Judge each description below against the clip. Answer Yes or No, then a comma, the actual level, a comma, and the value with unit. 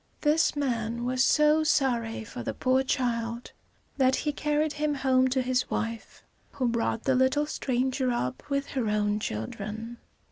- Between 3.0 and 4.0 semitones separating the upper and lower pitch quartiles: Yes, average, 3.3 semitones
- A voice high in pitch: Yes, very high, 255 Hz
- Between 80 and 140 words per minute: No, average, 155 wpm